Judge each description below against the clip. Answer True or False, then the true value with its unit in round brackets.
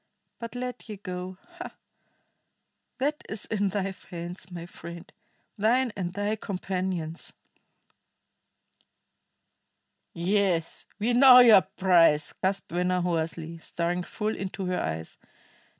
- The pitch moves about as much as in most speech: True (3.7 semitones)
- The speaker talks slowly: True (110 wpm)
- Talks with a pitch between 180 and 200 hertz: True (185 Hz)